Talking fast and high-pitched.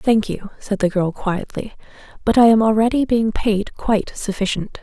No: average, 175 wpm; high, 215 Hz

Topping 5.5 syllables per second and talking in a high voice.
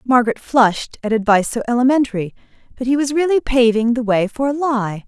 Yes: 6.1 syllables/s; high, 240 Hz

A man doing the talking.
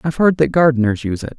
Yes: male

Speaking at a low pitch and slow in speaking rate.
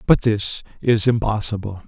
Yes: low, 105 Hz; slow, 130 wpm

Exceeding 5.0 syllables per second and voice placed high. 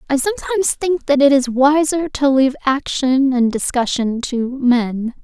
No: 4.5 syllables/s; very high, 270 Hz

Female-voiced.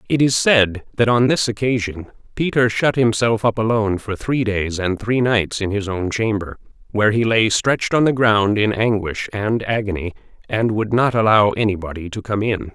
No: male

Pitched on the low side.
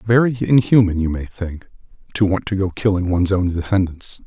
Yes: very low, 95 Hz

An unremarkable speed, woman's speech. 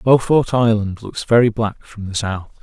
No: average, 185 wpm; male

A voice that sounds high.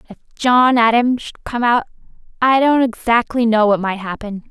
Yes: high, 235 Hz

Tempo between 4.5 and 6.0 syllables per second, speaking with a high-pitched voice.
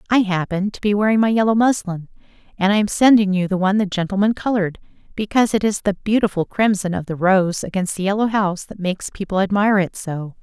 No: 6.4 syllables/s; high, 200 Hz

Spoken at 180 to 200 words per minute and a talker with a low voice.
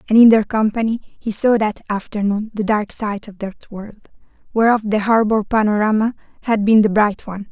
No: average, 185 wpm; high, 215 Hz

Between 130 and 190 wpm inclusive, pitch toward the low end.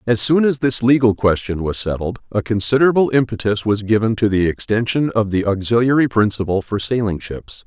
Yes: average, 180 wpm; low, 110 Hz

